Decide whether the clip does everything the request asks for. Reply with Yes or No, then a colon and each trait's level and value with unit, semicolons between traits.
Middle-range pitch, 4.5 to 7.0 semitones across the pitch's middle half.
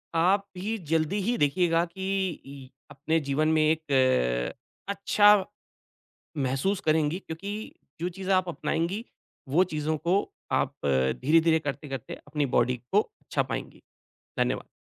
Yes: medium, 160 Hz; average, 5.0 semitones